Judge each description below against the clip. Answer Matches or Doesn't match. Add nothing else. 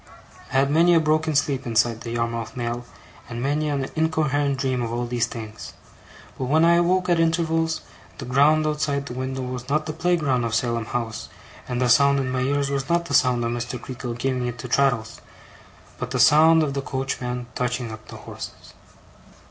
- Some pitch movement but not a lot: Matches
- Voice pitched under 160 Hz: Matches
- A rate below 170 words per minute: Doesn't match